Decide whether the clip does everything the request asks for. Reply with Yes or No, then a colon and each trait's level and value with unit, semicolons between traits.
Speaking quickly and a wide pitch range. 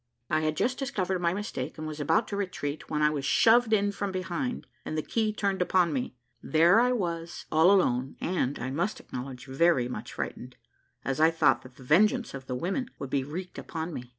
Yes: fast, 210 wpm; wide, 6.2 semitones